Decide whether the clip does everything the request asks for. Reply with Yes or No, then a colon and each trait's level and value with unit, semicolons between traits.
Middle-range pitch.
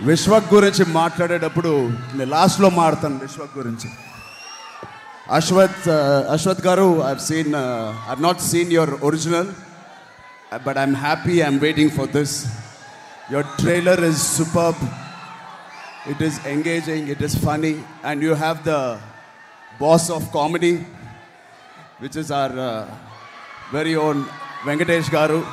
Yes: medium, 155 Hz